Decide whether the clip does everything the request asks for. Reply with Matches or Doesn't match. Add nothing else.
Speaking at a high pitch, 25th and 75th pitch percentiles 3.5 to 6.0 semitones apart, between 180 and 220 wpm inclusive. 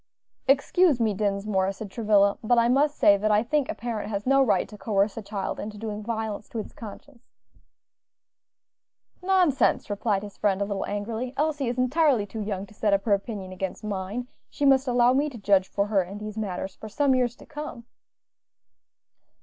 Matches